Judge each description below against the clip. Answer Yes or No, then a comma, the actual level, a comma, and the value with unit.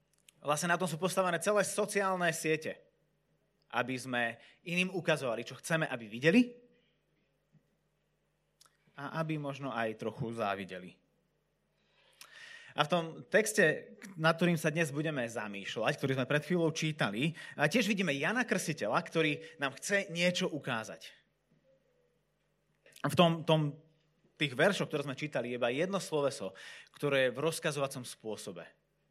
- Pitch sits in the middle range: Yes, medium, 155 Hz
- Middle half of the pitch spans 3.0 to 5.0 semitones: Yes, average, 4.7 semitones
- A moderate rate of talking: Yes, average, 130 wpm